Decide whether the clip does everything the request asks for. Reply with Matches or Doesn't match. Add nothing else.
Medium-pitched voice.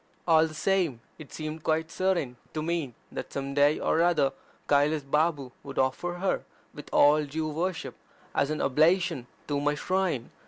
Matches